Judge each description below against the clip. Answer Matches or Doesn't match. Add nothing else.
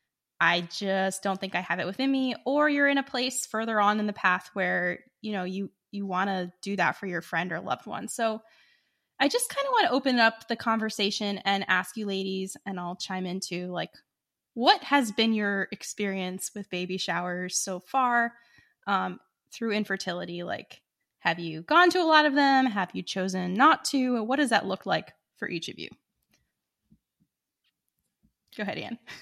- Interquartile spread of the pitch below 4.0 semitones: Doesn't match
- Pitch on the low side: Doesn't match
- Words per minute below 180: Doesn't match